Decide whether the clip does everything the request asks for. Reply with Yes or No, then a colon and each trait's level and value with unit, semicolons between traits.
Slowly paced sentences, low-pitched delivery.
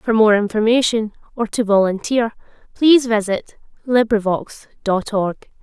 No: slow, 115 wpm; high, 220 Hz